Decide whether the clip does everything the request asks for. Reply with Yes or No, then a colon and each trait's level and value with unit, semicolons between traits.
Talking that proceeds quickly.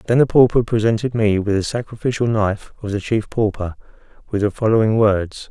No: average, 185 wpm